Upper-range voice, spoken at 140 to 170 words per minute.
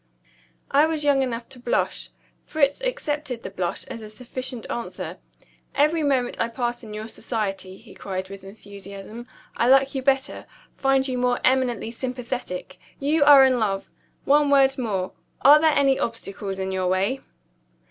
Yes: very high, 250 Hz; average, 160 wpm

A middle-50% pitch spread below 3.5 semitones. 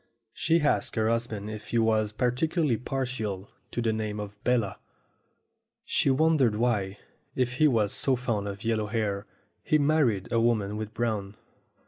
Yes: average, 3.1 semitones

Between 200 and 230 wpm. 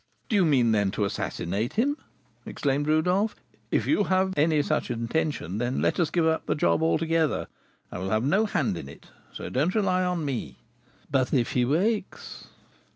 No: average, 180 wpm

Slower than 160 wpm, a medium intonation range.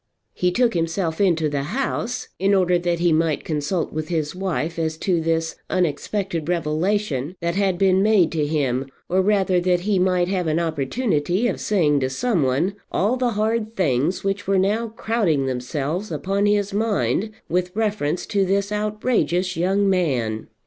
No: average, 170 wpm; average, 4.1 semitones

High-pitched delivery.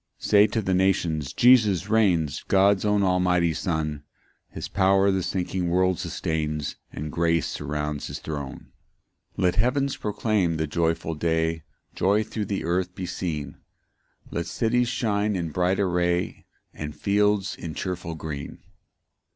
No: very low, 90 Hz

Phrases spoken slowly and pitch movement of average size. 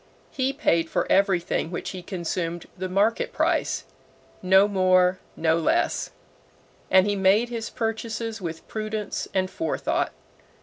Yes: slow, 130 wpm; average, 3.5 semitones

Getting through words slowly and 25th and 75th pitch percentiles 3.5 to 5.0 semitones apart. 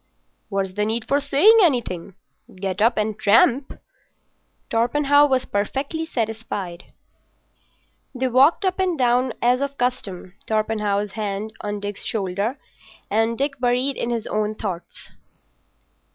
Yes: slow, 125 wpm; average, 4.6 semitones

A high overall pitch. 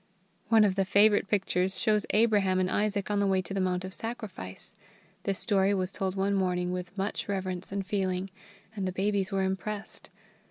Yes: high, 195 Hz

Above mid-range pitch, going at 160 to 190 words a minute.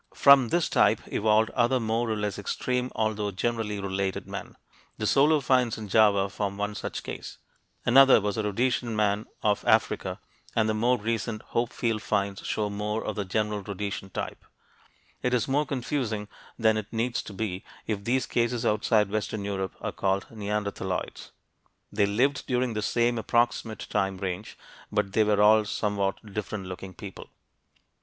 No: low, 110 Hz; average, 165 wpm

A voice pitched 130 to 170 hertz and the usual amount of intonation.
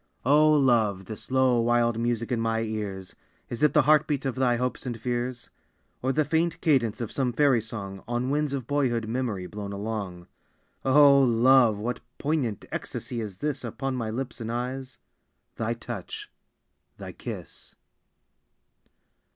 No: low, 120 Hz; average, 3.1 semitones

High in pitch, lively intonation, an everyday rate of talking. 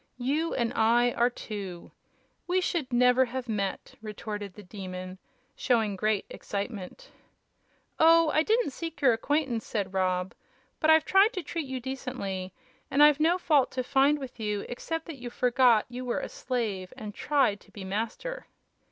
Yes: high, 245 Hz; wide, 6.0 semitones; average, 170 wpm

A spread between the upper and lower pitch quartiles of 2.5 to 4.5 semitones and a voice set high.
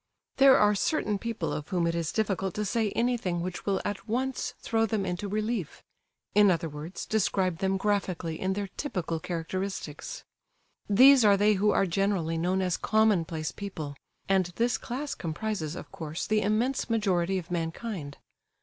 Yes: average, 4.2 semitones; high, 195 Hz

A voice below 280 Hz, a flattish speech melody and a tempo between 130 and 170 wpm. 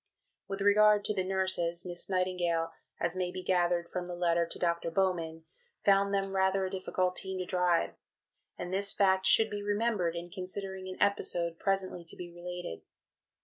No: medium, 185 Hz; narrow, 2.0 semitones; average, 180 wpm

